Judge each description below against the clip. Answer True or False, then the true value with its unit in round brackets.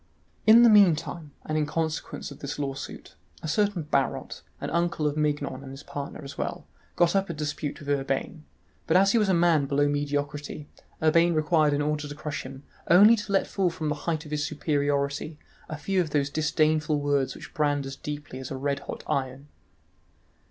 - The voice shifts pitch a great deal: False (2.5 semitones)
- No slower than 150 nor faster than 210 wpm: True (195 wpm)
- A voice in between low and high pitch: True (150 Hz)